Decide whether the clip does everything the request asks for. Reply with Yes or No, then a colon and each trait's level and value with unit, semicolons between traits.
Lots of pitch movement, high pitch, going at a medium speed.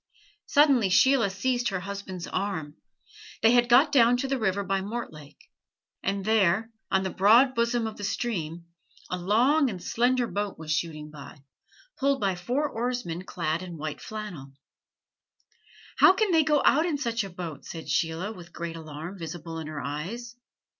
Yes: wide, 6.2 semitones; high, 200 Hz; average, 165 wpm